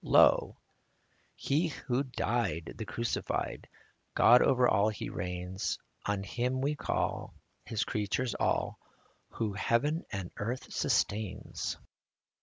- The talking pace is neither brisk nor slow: No, slow, 115 wpm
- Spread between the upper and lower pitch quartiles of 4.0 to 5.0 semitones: Yes, average, 4.4 semitones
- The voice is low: Yes, low, 115 Hz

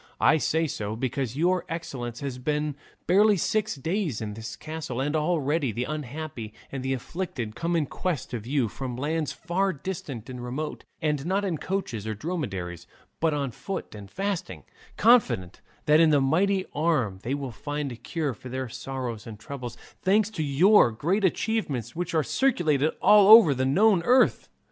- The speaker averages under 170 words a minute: No, average, 175 wpm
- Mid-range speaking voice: Yes, medium, 150 Hz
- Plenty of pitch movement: Yes, wide, 5.9 semitones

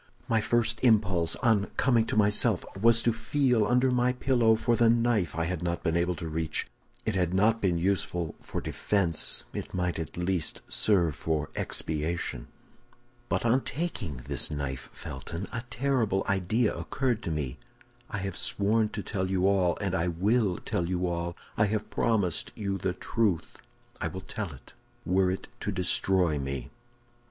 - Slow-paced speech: No, average, 170 wpm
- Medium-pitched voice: No, very low, 95 Hz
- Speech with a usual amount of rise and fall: Yes, average, 4.7 semitones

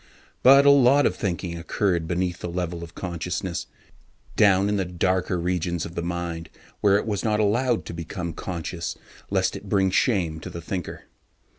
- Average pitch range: Yes, average, 3.0 semitones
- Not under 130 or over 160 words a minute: No, average, 180 wpm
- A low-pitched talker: Yes, very low, 90 Hz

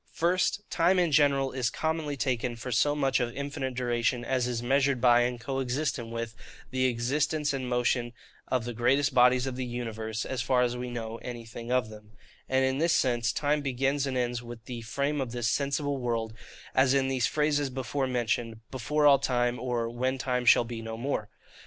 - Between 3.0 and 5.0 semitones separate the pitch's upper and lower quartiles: No, narrow, 2.5 semitones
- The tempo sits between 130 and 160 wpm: No, average, 195 wpm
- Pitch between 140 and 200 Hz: No, low, 125 Hz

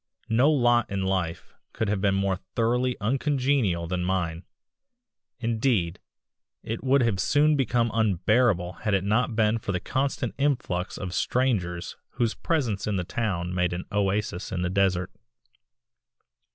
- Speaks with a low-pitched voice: Yes, low, 105 Hz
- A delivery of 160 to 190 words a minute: No, average, 145 wpm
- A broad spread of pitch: No, average, 4.8 semitones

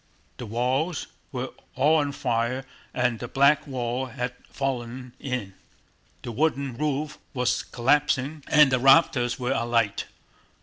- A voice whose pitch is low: Yes, low, 130 Hz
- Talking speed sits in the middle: No, slow, 130 wpm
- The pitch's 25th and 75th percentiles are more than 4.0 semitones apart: No, average, 2.8 semitones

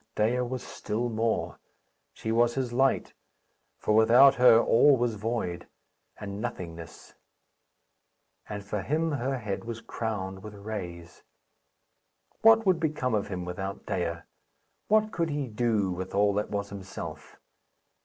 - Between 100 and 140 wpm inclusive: Yes, slow, 135 wpm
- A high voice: No, low, 110 Hz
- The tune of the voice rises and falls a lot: No, average, 4.1 semitones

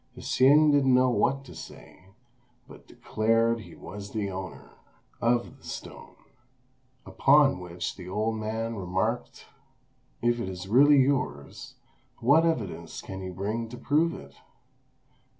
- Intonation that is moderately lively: No, wide, 5.7 semitones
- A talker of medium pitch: No, low, 115 Hz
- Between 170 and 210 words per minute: No, slow, 135 wpm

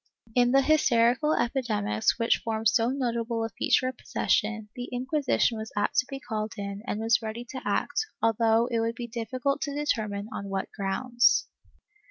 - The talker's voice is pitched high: Yes, high, 230 Hz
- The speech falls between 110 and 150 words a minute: No, average, 180 wpm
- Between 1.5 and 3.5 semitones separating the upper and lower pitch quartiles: Yes, average, 2.7 semitones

